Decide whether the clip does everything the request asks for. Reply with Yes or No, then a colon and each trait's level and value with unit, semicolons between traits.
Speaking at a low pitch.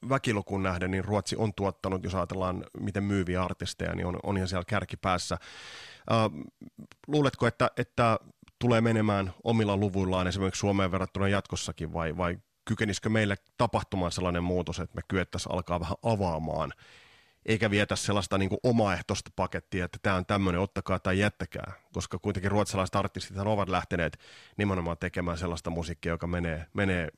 Yes: very low, 95 Hz